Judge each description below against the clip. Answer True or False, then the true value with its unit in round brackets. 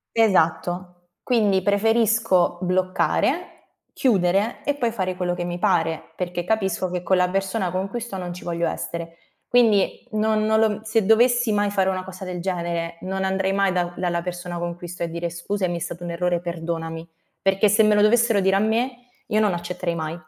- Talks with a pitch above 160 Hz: True (185 Hz)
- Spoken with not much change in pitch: False (3.4 semitones)